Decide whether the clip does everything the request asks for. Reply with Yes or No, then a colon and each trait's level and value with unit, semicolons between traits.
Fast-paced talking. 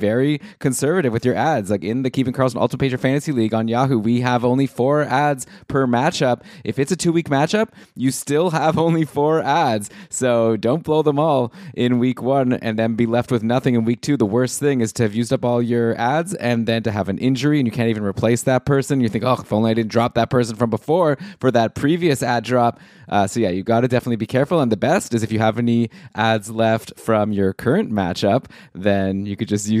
Yes: fast, 245 wpm